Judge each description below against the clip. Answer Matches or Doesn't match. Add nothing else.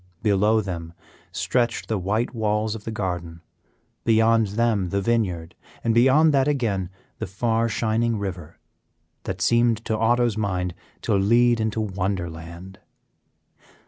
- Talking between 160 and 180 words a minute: Doesn't match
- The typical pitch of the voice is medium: Doesn't match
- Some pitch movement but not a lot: Matches